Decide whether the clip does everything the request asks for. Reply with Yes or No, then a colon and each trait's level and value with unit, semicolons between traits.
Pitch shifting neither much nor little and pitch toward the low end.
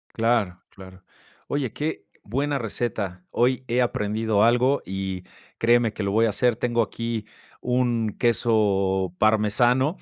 Yes: average, 3.2 semitones; low, 115 Hz